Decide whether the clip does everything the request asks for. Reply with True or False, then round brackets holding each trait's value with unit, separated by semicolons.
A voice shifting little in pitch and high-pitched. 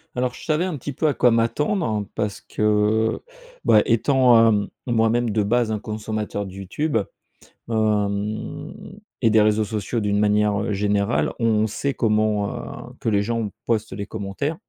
False (2.2 semitones; 110 Hz)